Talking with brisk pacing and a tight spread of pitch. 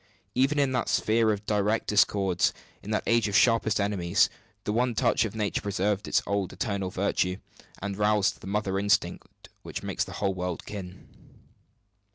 No: average, 170 wpm; narrow, 2.1 semitones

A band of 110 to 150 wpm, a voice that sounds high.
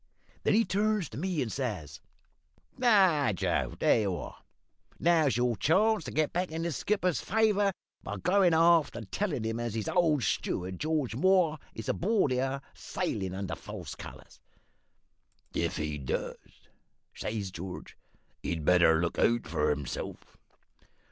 No: average, 145 wpm; low, 135 Hz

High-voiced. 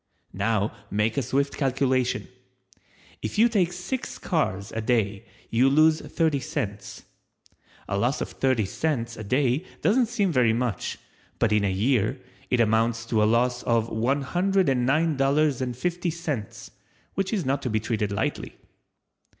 No: low, 125 Hz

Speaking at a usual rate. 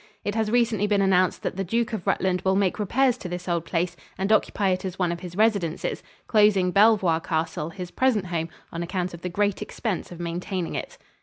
No: fast, 215 wpm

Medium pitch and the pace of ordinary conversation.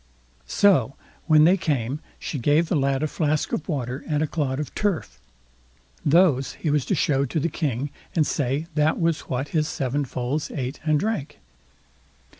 Yes: medium, 150 Hz; average, 175 wpm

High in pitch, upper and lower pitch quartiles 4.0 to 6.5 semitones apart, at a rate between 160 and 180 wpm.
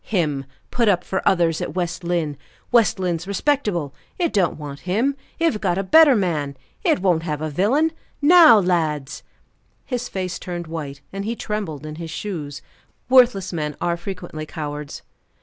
No: medium, 180 Hz; average, 5.3 semitones; average, 165 wpm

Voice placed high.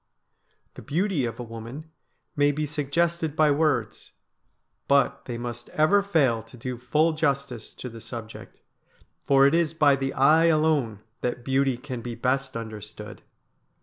No: low, 135 Hz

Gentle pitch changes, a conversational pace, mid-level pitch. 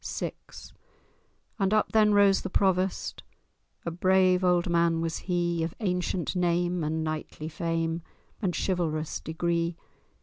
No: narrow, 2.1 semitones; slow, 130 wpm; medium, 175 Hz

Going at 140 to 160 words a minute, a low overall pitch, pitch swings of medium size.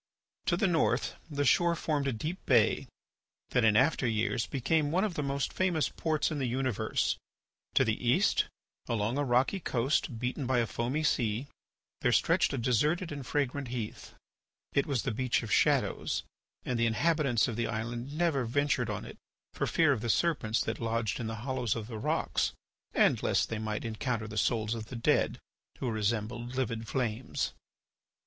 No: average, 180 wpm; low, 125 Hz; average, 4.1 semitones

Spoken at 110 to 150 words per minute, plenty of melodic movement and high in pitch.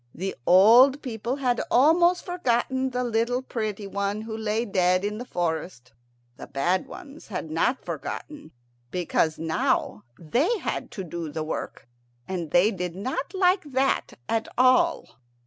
Yes: average, 145 wpm; wide, 6.5 semitones; high, 220 Hz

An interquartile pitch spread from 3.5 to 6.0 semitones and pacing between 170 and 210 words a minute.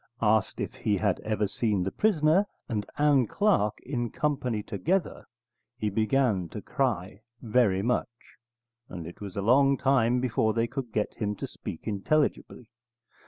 No: average, 4.7 semitones; average, 155 wpm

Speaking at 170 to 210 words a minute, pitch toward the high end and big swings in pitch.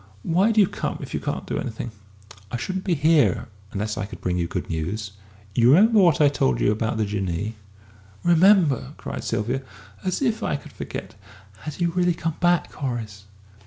No: average, 190 wpm; low, 135 Hz; wide, 8.8 semitones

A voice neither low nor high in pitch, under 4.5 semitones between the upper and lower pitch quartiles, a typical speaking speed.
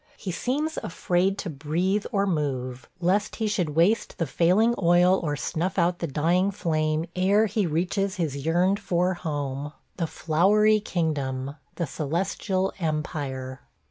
Yes: medium, 175 Hz; average, 4.1 semitones; average, 150 wpm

